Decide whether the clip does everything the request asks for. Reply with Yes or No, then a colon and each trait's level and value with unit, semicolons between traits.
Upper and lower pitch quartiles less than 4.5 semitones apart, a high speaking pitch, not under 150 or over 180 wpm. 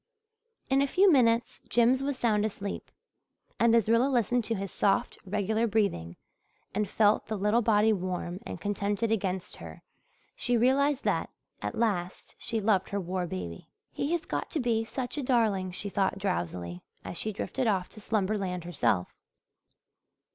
Yes: average, 3.9 semitones; high, 210 Hz; average, 160 wpm